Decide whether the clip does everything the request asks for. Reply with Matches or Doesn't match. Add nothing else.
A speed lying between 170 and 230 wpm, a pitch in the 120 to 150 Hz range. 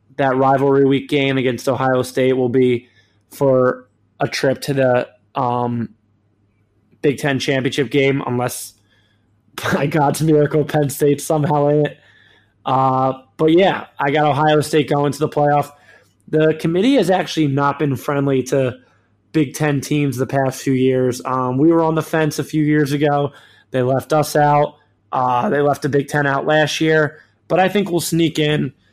Matches